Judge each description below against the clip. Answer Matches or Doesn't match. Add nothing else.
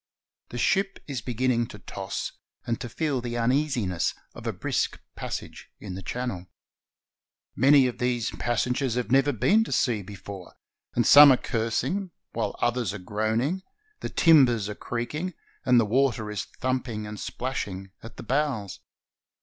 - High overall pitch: Doesn't match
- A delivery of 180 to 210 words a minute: Doesn't match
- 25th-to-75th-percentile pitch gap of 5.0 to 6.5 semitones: Doesn't match